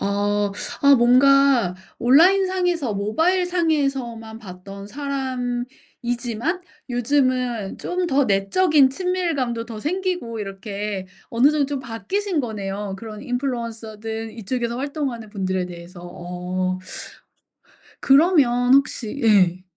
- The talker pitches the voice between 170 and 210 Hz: No, high, 240 Hz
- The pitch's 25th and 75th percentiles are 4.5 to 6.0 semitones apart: Yes, wide, 5.4 semitones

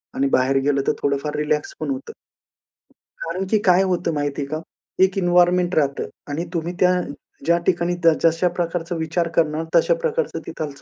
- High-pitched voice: No, medium, 165 Hz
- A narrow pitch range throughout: No, average, 3.1 semitones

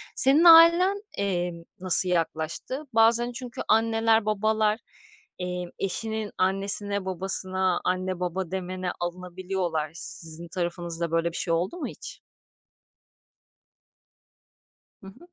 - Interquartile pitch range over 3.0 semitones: Yes, average, 3.9 semitones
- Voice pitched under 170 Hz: No, high, 190 Hz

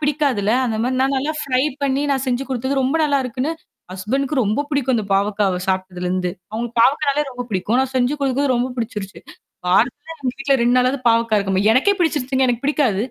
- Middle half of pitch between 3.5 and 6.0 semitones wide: Yes, average, 4.1 semitones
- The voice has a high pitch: Yes, very high, 255 Hz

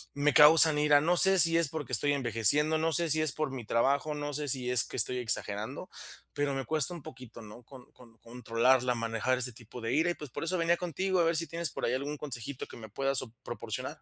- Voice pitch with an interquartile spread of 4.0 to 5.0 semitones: Yes, average, 4.3 semitones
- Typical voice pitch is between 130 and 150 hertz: Yes, medium, 140 Hz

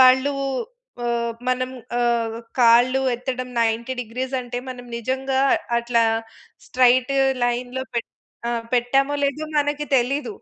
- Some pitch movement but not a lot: No, narrow, 1.8 semitones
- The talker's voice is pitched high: Yes, very high, 250 Hz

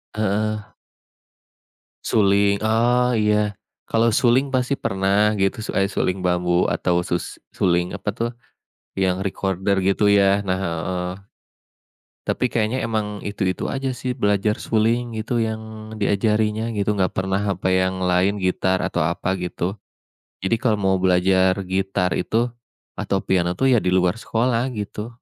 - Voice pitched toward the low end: Yes, low, 100 Hz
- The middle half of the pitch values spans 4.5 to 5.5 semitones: No, average, 3.0 semitones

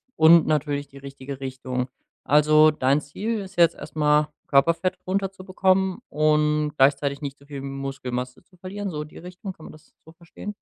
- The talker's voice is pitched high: No, medium, 150 Hz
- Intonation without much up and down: No, average, 4.6 semitones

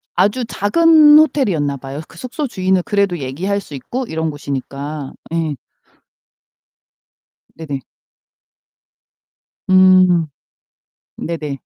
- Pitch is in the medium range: Yes, medium, 175 Hz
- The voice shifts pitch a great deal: Yes, wide, 5.8 semitones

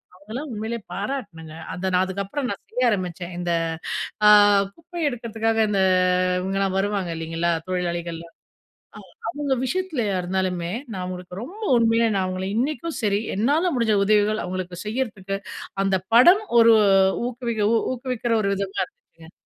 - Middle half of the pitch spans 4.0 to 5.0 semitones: Yes, average, 4.7 semitones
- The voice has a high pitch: Yes, high, 205 Hz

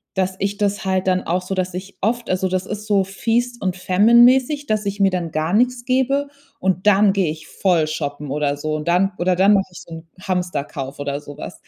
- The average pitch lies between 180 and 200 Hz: Yes, high, 190 Hz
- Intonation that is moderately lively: Yes, average, 3.4 semitones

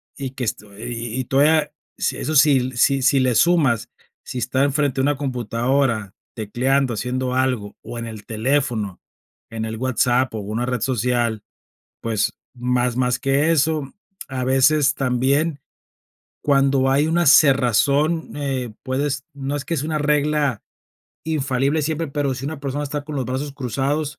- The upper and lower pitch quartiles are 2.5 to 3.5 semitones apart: Yes, average, 3.0 semitones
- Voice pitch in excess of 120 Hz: Yes, low, 135 Hz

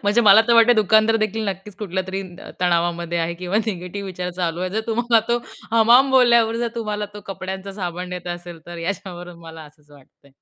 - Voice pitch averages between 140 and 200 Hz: Yes, high, 190 Hz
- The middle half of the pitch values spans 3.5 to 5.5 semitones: Yes, average, 4.1 semitones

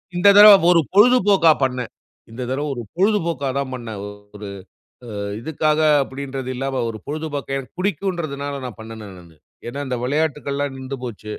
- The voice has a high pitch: No, medium, 140 Hz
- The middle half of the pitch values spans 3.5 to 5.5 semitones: Yes, average, 4.3 semitones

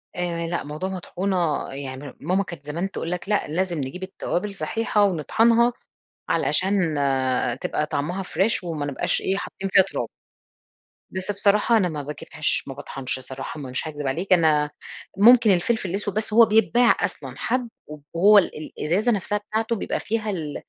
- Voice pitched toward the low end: No, medium, 185 Hz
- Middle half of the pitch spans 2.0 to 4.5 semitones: No, average, 5.3 semitones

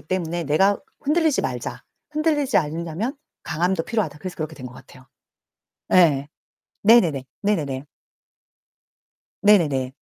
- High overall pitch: No, medium, 170 Hz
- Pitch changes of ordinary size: No, wide, 6.1 semitones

